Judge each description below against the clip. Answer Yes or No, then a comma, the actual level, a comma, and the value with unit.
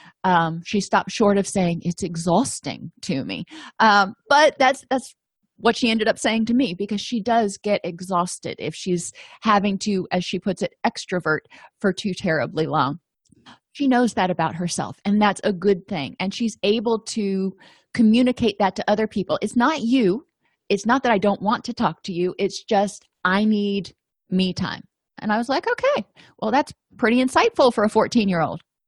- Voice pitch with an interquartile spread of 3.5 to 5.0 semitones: Yes, average, 3.8 semitones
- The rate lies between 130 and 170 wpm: No, average, 185 wpm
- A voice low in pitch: No, high, 200 Hz